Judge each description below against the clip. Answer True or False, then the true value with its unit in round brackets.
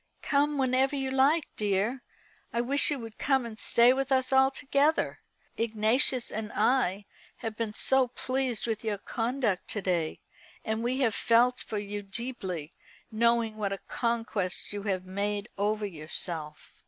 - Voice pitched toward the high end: True (230 Hz)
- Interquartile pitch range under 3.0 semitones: False (4.2 semitones)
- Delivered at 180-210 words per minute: False (155 wpm)